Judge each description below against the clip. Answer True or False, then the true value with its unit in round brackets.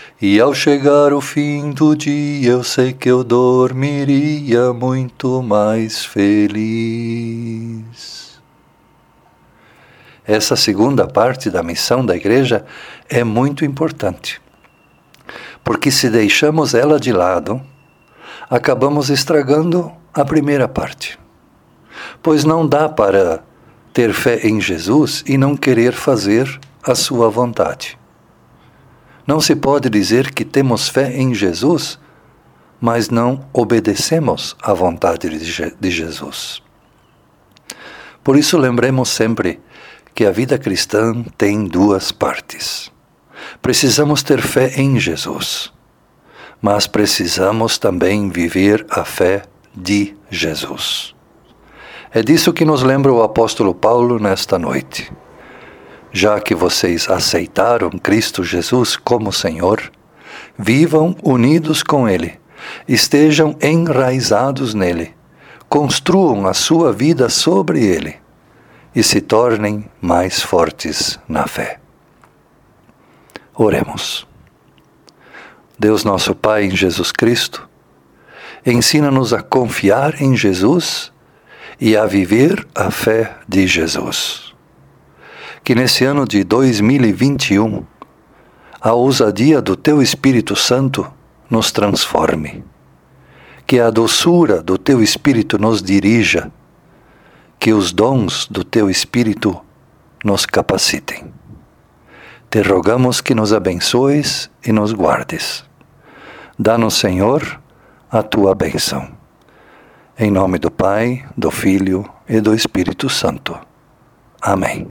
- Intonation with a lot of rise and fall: False (5.0 semitones)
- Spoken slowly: True (105 wpm)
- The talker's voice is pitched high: False (120 Hz)